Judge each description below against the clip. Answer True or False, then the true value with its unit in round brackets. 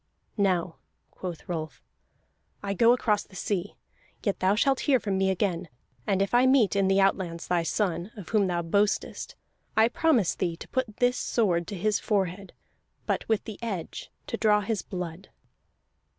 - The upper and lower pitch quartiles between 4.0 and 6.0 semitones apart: False (3.4 semitones)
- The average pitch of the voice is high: True (195 Hz)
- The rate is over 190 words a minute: False (175 wpm)